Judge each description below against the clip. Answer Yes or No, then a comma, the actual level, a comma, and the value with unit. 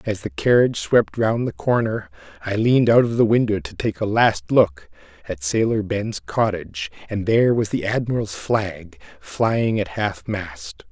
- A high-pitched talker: No, low, 110 Hz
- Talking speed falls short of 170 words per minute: No, average, 175 wpm